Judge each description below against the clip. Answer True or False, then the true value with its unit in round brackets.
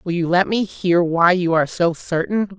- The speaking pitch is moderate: True (175 Hz)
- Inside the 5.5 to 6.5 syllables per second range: False (4.9 syllables/s)